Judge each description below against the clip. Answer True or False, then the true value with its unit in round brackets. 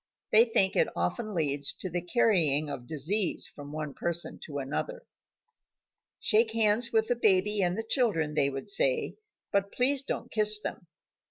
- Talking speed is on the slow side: False (170 wpm)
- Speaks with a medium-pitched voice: False (200 Hz)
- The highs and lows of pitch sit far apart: True (6.7 semitones)